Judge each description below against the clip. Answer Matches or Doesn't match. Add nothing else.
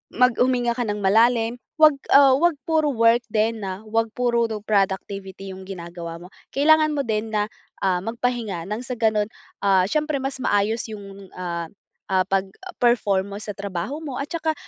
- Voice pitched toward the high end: Matches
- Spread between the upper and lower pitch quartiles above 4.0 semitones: Matches